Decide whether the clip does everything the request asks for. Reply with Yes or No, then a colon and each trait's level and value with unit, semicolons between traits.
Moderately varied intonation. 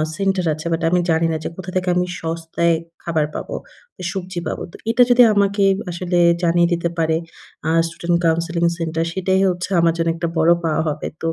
No: narrow, 1.9 semitones